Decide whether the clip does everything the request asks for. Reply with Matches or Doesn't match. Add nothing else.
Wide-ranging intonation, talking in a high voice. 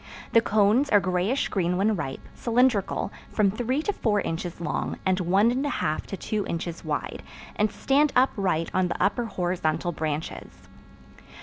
Doesn't match